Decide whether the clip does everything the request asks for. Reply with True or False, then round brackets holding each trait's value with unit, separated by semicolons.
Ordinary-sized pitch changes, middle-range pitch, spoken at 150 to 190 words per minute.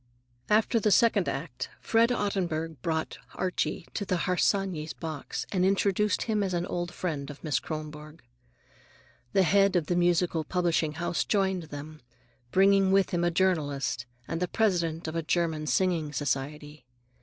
True (3.7 semitones; 175 Hz; 155 wpm)